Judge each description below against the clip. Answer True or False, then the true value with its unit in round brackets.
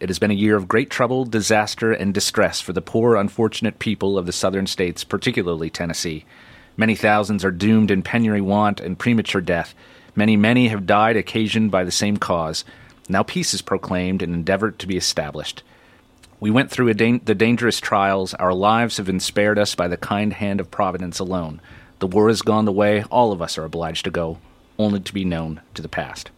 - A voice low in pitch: True (100 Hz)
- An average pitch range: True (3.1 semitones)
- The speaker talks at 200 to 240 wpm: True (205 wpm)